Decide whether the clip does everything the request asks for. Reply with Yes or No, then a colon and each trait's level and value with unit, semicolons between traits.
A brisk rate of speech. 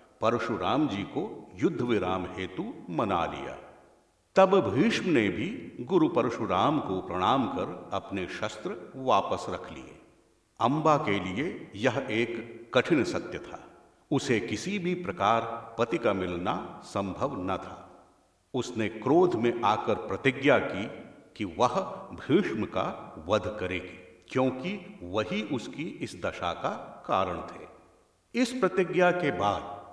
No: average, 130 wpm